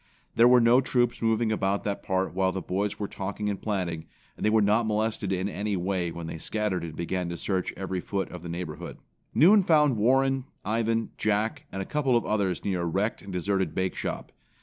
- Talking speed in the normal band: No, fast, 210 wpm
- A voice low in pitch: Yes, low, 100 Hz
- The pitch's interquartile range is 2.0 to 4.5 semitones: Yes, average, 3.5 semitones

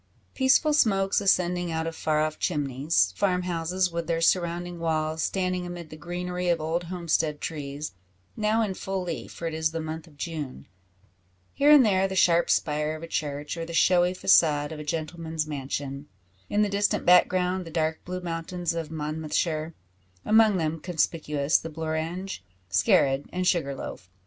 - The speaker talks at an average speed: Yes, average, 170 wpm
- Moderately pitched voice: Yes, medium, 165 Hz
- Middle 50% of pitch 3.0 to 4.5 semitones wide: No, narrow, 2.6 semitones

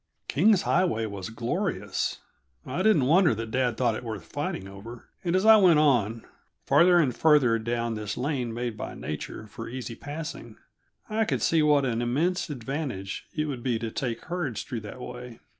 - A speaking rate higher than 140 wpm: Yes, average, 180 wpm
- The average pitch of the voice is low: Yes, low, 125 Hz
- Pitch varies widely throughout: Yes, wide, 5.8 semitones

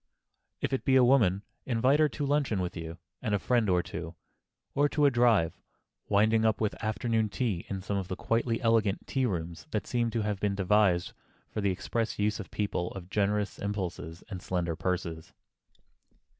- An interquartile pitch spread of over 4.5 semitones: No, average, 4.0 semitones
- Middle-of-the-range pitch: No, low, 105 Hz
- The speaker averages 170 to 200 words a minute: Yes, average, 185 wpm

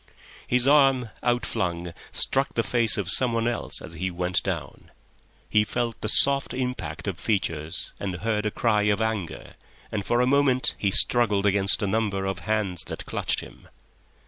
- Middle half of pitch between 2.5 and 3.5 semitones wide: No, average, 4.0 semitones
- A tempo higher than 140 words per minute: Yes, average, 170 wpm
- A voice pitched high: No, low, 110 Hz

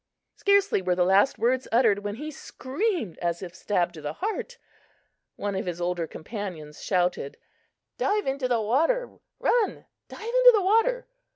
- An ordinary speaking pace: Yes, average, 160 wpm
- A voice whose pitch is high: Yes, high, 225 Hz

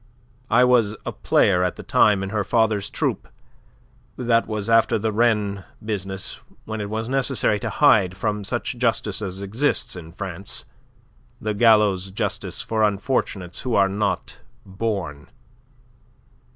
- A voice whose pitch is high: No, low, 105 Hz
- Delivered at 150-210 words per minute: No, average, 140 wpm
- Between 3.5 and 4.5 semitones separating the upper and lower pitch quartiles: No, average, 2.8 semitones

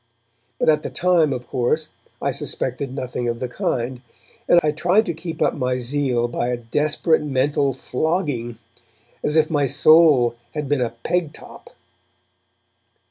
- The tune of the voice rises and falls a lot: No, average, 4.0 semitones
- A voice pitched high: No, medium, 140 Hz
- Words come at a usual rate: Yes, average, 155 wpm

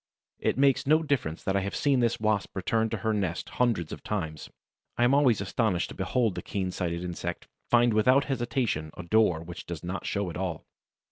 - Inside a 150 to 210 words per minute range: Yes, fast, 205 wpm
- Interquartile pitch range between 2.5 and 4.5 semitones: No, average, 5.2 semitones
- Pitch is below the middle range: Yes, low, 105 Hz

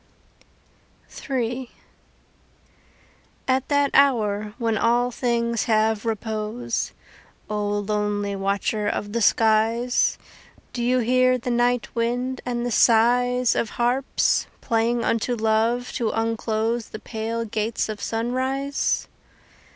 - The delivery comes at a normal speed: No, slow, 110 wpm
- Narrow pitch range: Yes, narrow, 2.2 semitones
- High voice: Yes, high, 230 Hz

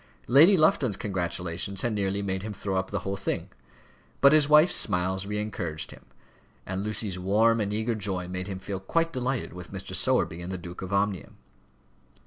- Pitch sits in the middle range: No, low, 100 Hz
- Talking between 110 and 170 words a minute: No, average, 185 wpm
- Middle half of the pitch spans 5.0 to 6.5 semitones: No, average, 3.0 semitones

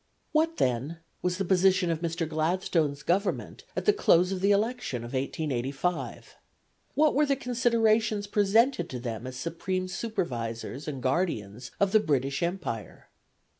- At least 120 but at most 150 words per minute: Yes, average, 145 wpm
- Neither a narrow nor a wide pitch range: No, wide, 7.0 semitones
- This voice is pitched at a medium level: Yes, medium, 175 Hz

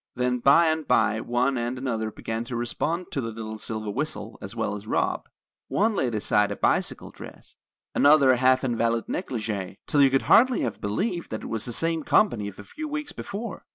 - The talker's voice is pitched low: Yes, low, 120 Hz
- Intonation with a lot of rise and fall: Yes, wide, 5.8 semitones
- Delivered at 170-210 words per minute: Yes, average, 200 wpm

